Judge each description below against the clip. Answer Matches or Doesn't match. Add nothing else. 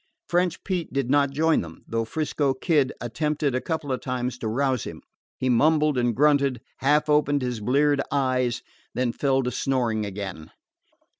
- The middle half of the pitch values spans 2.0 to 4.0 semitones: Matches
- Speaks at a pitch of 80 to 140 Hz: Matches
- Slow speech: Doesn't match